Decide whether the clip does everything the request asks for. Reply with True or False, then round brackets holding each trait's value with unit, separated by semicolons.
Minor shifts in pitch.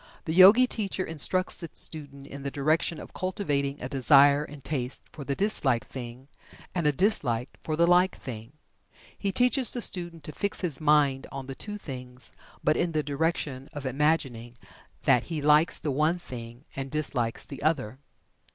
False (4.1 semitones)